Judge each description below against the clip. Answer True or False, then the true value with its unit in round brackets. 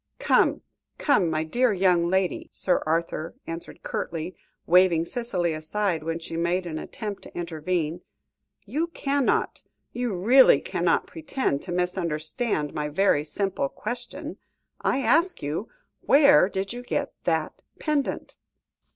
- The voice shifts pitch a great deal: True (6.7 semitones)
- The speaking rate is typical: False (130 wpm)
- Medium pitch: True (180 Hz)